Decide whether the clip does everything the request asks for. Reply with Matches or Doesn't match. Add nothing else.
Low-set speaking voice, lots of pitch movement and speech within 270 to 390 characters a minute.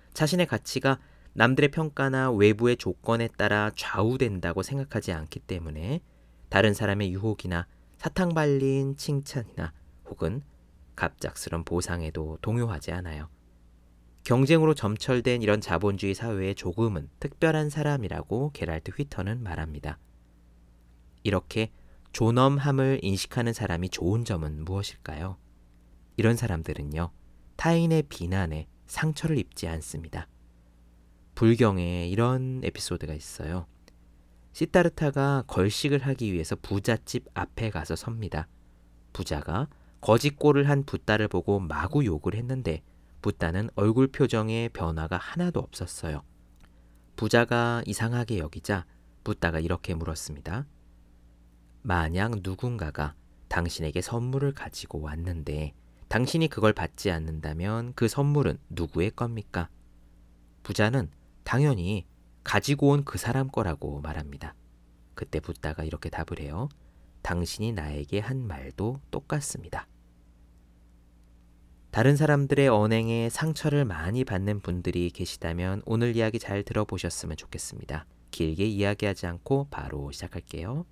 Matches